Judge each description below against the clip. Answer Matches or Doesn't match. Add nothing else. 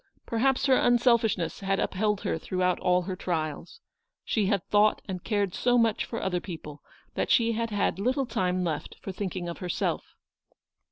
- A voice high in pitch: Matches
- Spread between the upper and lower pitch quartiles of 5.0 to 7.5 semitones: Doesn't match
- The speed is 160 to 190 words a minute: Matches